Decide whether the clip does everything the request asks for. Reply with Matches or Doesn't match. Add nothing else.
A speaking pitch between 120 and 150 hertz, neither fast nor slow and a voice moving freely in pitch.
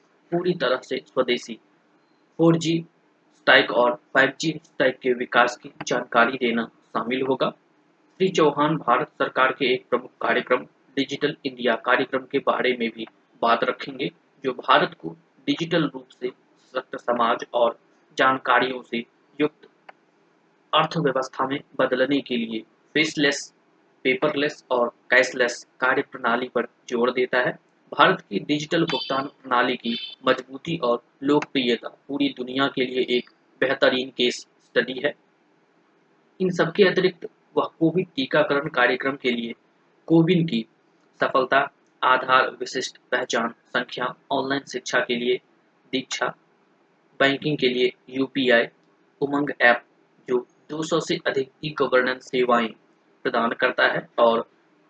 Doesn't match